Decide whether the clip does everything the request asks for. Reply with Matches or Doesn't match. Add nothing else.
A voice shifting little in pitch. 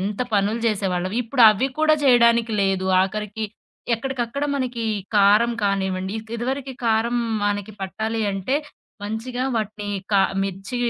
Doesn't match